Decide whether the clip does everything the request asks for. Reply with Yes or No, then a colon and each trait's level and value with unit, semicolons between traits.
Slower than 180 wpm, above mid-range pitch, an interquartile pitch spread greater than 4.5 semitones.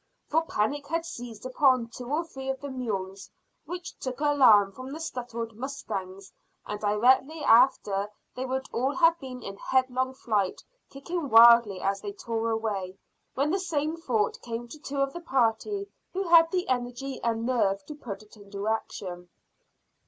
Yes: average, 165 wpm; very high, 250 Hz; average, 5.0 semitones